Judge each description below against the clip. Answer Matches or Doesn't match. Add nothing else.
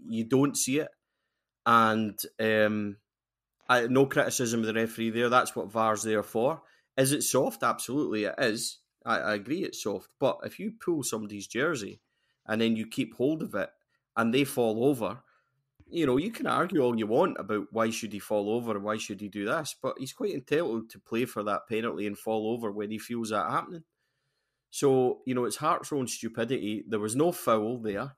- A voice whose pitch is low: Matches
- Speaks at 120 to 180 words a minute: Doesn't match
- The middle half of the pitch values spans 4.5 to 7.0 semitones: Doesn't match